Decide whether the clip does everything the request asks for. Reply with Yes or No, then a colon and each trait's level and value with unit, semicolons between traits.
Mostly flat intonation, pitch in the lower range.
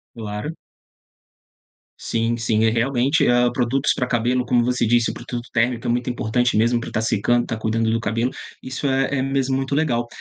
Yes: narrow, 2.0 semitones; low, 120 Hz